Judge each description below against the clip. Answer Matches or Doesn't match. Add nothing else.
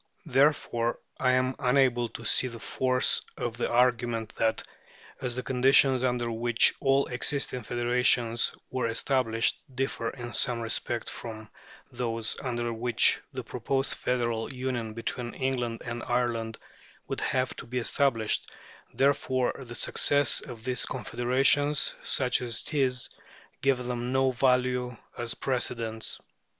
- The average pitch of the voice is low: Matches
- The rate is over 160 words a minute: Doesn't match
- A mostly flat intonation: Matches